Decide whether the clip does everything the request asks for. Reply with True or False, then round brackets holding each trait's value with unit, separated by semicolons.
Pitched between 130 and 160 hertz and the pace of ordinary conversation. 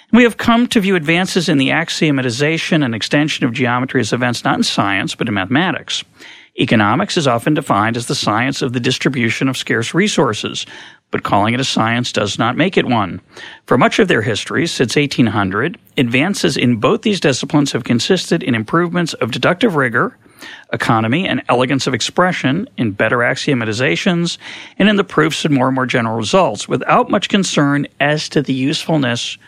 True (140 Hz; 180 wpm)